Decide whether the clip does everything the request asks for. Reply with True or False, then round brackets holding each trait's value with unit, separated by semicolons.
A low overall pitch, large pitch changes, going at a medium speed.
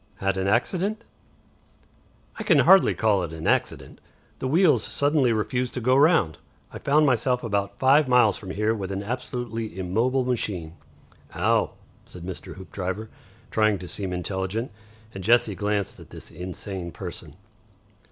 False (105 Hz; 5.0 semitones; 150 wpm)